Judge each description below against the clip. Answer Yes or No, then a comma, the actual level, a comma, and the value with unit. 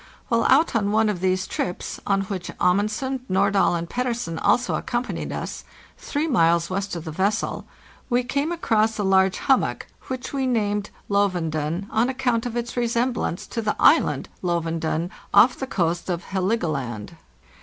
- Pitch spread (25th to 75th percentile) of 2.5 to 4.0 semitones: No, average, 5.3 semitones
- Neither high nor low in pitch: No, high, 205 Hz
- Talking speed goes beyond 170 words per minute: No, average, 160 wpm